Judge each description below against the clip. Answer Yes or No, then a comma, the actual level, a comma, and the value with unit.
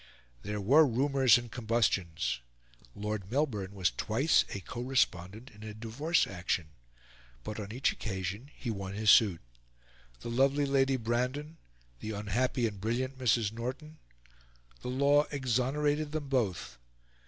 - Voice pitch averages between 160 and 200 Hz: No, low, 120 Hz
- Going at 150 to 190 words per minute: No, slow, 135 wpm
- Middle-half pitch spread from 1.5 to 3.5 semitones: No, average, 4.6 semitones